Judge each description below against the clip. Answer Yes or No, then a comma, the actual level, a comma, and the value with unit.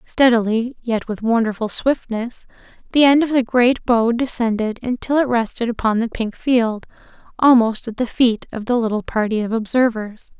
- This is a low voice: No, high, 235 Hz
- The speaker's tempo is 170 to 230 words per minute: No, average, 160 wpm